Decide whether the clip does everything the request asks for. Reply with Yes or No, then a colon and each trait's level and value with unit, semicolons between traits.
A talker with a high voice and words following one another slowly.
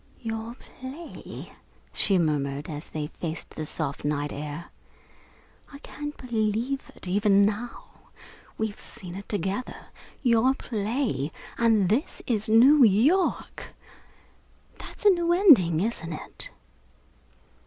Yes: high, 215 Hz; slow, 115 wpm